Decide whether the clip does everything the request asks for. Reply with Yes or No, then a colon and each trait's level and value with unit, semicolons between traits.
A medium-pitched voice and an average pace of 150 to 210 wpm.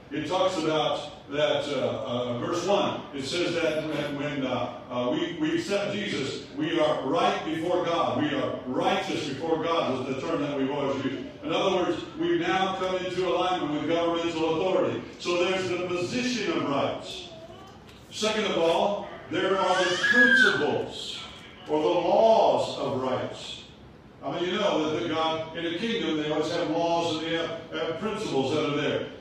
Yes: medium, 170 Hz; average, 180 wpm